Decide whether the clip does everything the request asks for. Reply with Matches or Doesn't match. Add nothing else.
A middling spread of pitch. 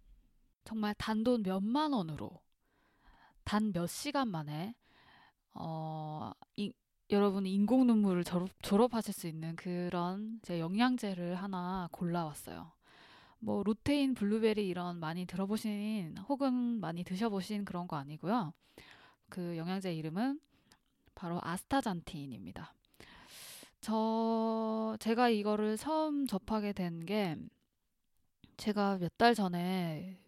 Matches